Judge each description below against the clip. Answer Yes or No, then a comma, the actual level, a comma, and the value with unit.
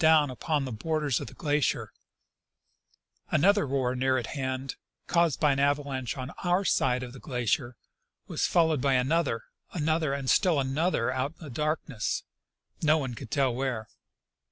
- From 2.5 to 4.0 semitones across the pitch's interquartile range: Yes, average, 3.5 semitones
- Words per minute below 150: No, average, 175 wpm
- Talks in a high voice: No, medium, 140 Hz